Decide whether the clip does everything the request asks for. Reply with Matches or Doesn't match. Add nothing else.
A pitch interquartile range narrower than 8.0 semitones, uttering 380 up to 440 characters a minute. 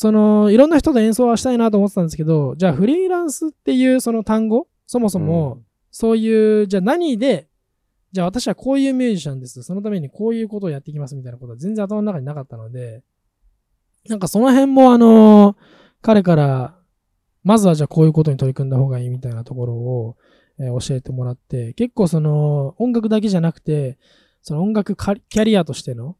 Doesn't match